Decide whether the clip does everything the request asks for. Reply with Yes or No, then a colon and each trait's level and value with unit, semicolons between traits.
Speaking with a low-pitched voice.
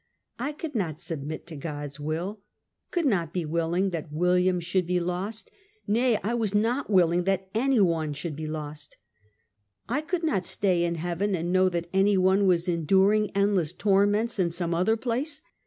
No: medium, 185 Hz